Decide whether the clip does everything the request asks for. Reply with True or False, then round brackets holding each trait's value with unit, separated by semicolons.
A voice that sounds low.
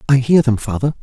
True (130 Hz)